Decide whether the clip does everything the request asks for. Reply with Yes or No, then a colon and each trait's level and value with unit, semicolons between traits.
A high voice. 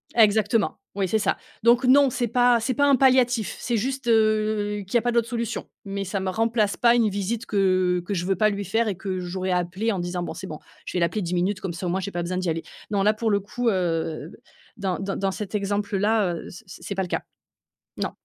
Yes: high, 205 Hz